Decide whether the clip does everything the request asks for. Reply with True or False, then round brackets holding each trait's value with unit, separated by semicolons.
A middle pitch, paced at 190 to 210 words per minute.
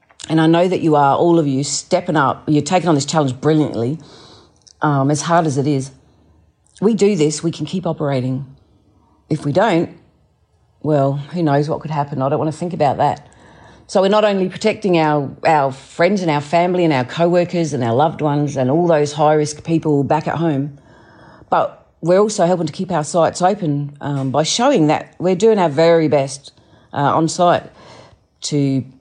True (150 Hz; 200 wpm)